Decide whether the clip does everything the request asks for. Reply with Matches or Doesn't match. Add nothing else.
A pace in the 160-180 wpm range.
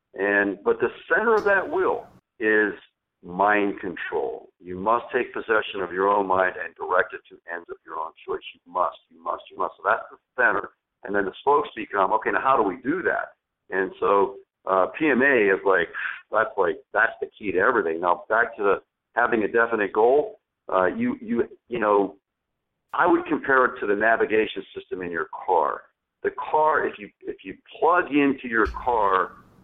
Doesn't match